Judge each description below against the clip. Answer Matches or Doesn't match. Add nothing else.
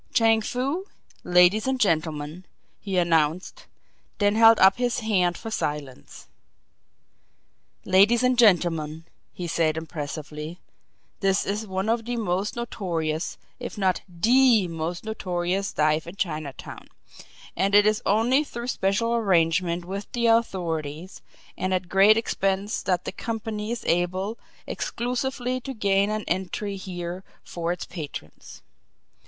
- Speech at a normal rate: Doesn't match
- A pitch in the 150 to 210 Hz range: Matches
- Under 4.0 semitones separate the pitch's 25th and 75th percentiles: Doesn't match